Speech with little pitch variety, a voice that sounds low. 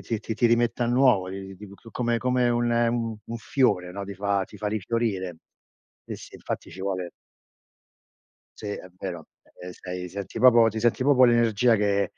No: average, 3.5 semitones; low, 110 Hz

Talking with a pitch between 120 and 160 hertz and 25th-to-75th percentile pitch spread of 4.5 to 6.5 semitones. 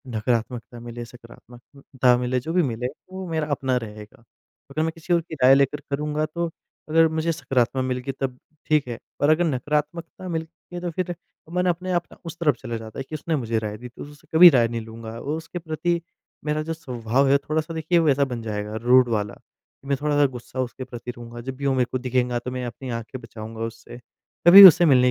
Yes: low, 135 Hz; average, 4.8 semitones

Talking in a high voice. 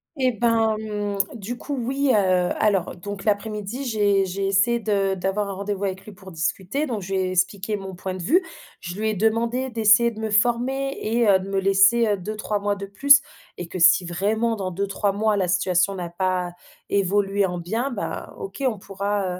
Yes: high, 200 Hz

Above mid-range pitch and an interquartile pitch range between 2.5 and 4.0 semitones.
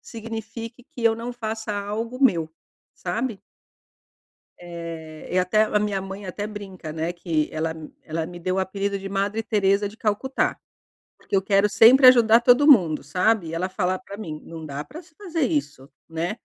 No: high, 200 Hz; average, 4.5 semitones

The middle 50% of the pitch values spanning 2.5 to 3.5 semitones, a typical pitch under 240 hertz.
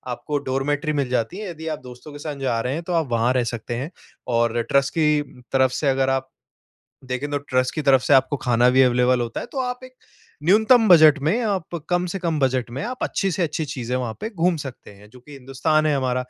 No: average, 4.4 semitones; medium, 140 Hz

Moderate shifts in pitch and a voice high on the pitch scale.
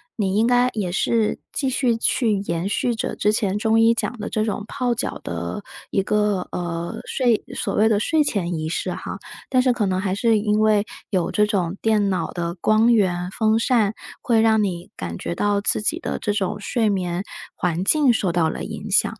Yes: average, 3.5 semitones; high, 210 Hz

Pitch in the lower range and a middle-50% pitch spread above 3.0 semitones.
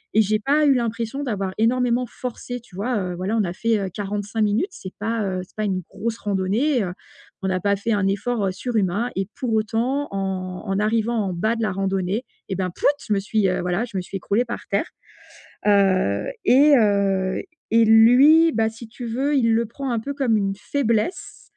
No: high, 215 Hz; average, 3.6 semitones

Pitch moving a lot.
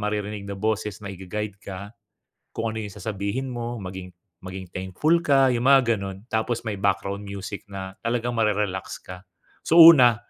No: average, 3.2 semitones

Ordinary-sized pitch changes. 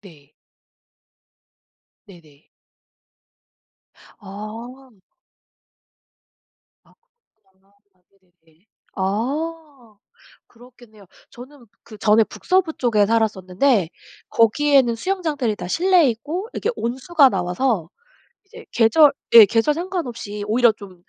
No: wide, 6.0 semitones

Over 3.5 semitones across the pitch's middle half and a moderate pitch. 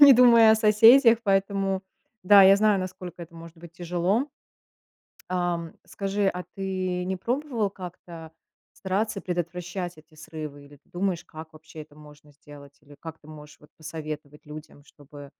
Yes: average, 4.1 semitones; medium, 175 Hz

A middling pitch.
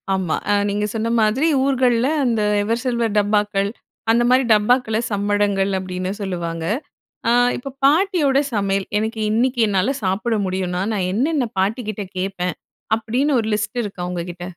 No: high, 210 Hz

